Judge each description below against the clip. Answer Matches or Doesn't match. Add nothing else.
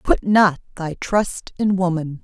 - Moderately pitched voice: Matches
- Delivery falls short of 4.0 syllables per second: Matches